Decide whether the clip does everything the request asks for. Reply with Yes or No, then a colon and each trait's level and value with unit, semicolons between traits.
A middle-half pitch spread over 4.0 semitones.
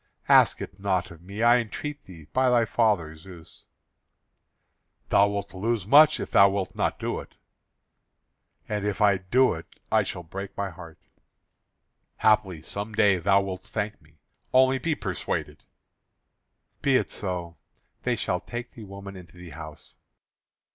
No: average, 3.7 semitones